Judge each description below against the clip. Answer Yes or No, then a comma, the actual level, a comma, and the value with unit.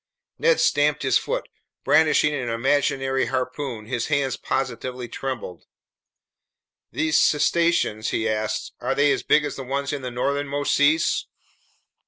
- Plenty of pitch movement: No, average, 2.7 semitones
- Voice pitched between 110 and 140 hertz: Yes, low, 135 Hz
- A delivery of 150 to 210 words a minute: No, slow, 135 wpm